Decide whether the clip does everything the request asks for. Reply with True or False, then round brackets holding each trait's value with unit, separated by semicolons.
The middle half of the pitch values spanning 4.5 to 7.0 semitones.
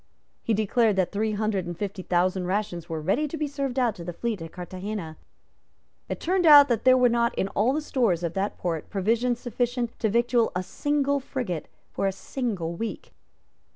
True (5.2 semitones)